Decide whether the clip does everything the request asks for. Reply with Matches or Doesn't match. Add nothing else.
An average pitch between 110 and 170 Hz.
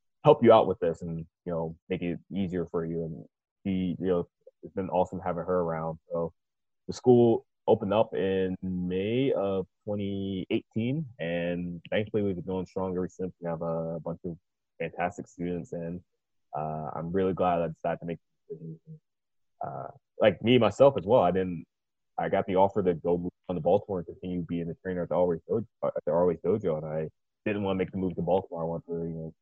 Doesn't match